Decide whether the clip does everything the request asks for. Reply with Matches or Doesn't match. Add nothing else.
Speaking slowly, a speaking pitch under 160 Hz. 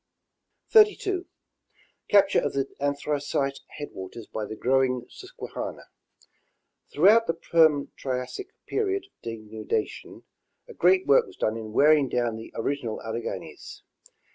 Matches